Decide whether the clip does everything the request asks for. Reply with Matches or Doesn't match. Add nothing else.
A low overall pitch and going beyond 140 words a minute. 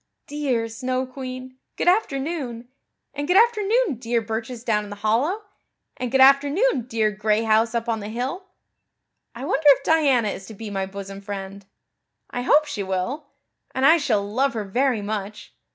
Doesn't match